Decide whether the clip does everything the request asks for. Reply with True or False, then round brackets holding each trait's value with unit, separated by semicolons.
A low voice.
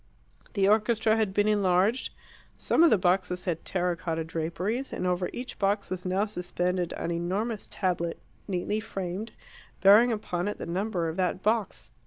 False (190 Hz)